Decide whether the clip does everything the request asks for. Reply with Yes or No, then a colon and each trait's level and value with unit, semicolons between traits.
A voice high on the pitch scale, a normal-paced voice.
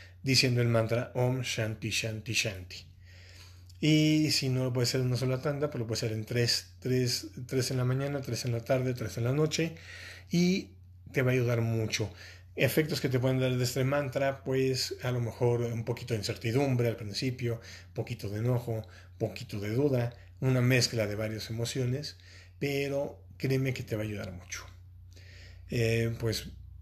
No: low, 115 Hz; average, 185 wpm